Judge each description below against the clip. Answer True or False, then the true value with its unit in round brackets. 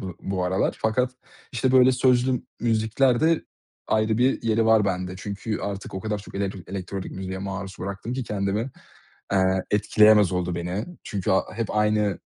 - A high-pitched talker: False (105 Hz)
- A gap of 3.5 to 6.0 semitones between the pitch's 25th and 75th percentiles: False (3.0 semitones)